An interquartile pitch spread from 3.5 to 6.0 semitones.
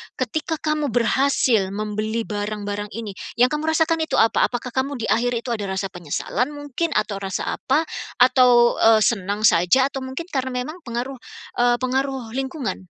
Yes: average, 4.1 semitones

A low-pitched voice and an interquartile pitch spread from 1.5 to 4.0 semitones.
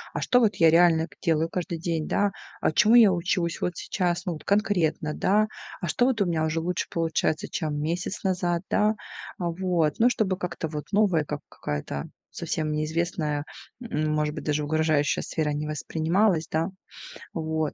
No: medium, 165 Hz; average, 3.1 semitones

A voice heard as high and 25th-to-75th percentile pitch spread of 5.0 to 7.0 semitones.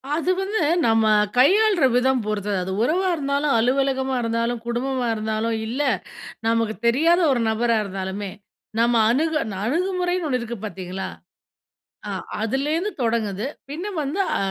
Yes: very high, 250 Hz; wide, 5.5 semitones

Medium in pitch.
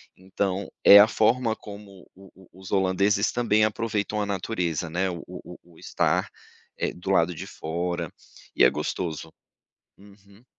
No: very low, 95 Hz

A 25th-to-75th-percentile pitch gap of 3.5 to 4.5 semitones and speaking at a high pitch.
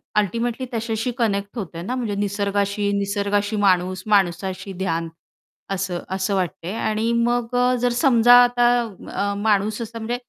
No: average, 2.9 semitones; high, 205 Hz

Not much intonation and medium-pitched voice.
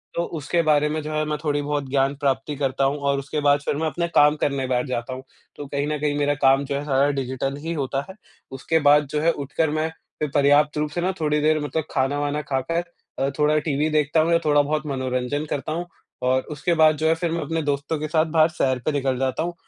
Yes: narrow, 2.0 semitones; medium, 145 Hz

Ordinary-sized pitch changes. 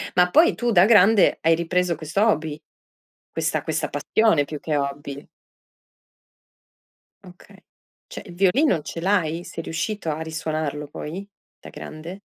Yes: average, 3.8 semitones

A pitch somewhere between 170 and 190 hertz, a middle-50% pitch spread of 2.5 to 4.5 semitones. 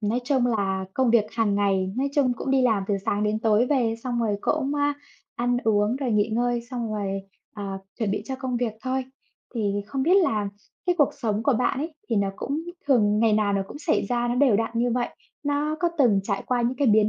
No: high, 235 Hz; average, 4.0 semitones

